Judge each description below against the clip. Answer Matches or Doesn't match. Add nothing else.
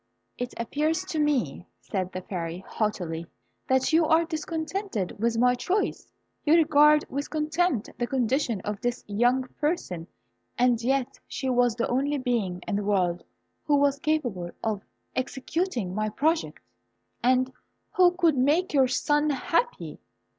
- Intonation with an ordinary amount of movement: Doesn't match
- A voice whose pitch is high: Matches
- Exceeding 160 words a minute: Doesn't match